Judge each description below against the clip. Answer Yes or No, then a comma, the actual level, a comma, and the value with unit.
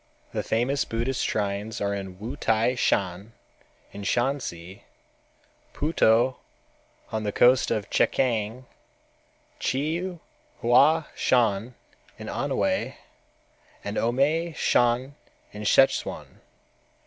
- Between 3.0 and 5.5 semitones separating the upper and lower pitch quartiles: Yes, average, 4.3 semitones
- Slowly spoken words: Yes, slow, 90 wpm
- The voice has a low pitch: Yes, low, 120 Hz